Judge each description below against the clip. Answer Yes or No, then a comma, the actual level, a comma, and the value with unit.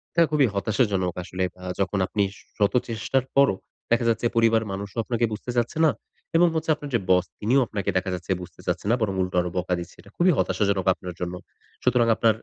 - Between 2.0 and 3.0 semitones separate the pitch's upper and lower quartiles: No, average, 4.1 semitones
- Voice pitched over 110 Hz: No, low, 105 Hz